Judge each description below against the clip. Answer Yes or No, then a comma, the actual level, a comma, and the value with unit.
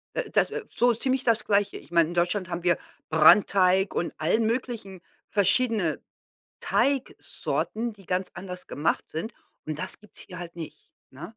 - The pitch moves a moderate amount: Yes, average, 4.7 semitones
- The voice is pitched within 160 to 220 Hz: Yes, high, 190 Hz